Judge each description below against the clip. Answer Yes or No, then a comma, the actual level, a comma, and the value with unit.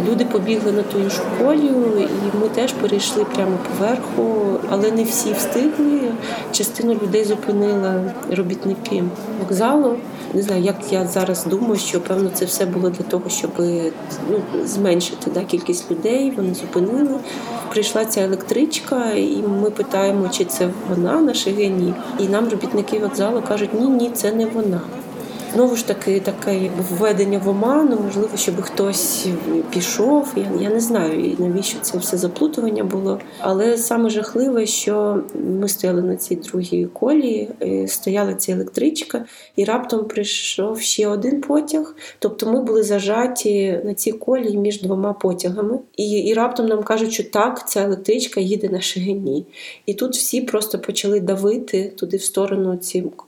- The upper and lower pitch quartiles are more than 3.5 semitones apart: No, average, 3.2 semitones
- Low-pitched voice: No, high, 210 Hz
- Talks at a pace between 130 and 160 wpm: Yes, average, 150 wpm